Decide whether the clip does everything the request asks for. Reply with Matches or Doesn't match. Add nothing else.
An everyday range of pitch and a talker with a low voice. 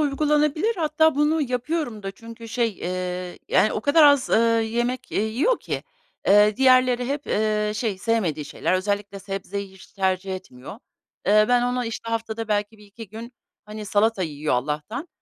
Doesn't match